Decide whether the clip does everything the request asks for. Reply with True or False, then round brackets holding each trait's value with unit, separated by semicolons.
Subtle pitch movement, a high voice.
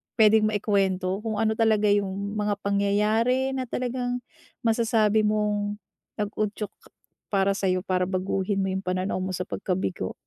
True (2.2 semitones; 205 Hz)